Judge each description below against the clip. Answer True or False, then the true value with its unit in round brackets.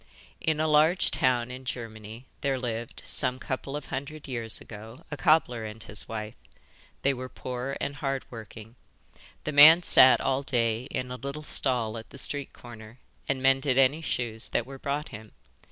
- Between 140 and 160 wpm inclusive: False (175 wpm)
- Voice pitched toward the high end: False (130 Hz)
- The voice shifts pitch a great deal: False (3.4 semitones)